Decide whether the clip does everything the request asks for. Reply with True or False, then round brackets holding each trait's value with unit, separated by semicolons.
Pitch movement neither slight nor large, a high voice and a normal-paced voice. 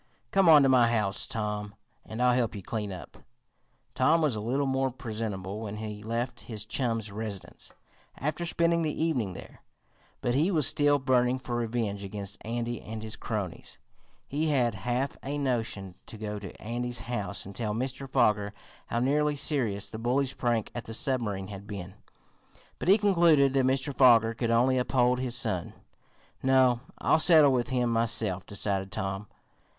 False (4.0 semitones; 120 Hz; 170 wpm)